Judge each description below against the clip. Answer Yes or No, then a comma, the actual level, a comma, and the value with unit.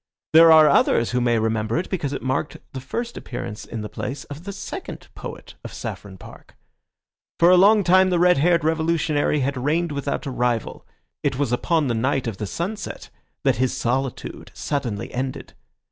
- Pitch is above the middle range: No, medium, 140 Hz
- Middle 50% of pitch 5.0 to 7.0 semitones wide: Yes, wide, 5.4 semitones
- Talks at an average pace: Yes, average, 185 wpm